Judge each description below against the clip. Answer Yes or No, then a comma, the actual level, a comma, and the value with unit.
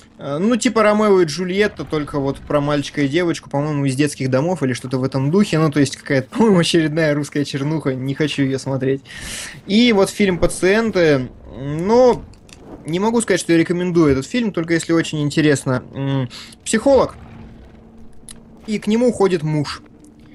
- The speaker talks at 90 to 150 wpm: No, fast, 160 wpm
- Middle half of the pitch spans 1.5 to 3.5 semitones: No, wide, 5.6 semitones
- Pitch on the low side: No, medium, 155 Hz